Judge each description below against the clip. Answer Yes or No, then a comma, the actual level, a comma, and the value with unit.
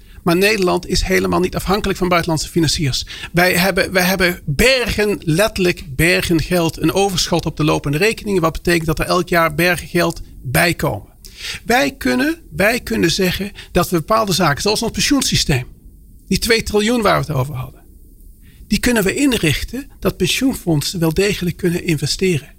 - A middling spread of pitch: Yes, average, 3.9 semitones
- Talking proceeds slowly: No, average, 160 wpm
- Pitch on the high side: No, medium, 180 Hz